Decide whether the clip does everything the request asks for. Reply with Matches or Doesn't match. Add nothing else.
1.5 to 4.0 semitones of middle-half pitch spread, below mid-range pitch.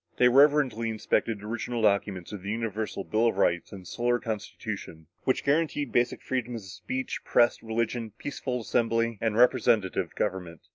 Matches